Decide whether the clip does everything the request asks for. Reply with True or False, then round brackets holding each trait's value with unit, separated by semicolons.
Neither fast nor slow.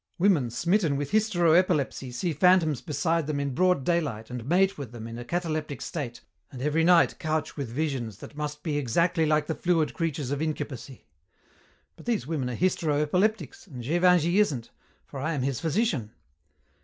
True (180 wpm)